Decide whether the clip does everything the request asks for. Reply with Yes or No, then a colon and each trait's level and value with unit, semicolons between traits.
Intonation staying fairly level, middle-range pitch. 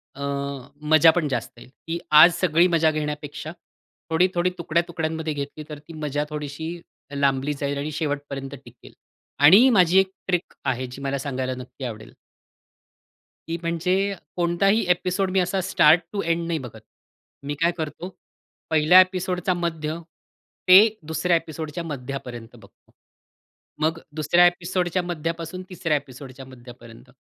No: average, 3.8 semitones; medium, 160 Hz